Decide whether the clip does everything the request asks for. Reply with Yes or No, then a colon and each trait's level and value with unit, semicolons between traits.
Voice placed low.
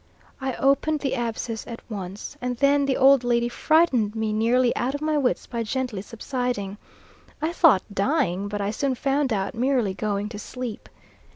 No: high, 245 Hz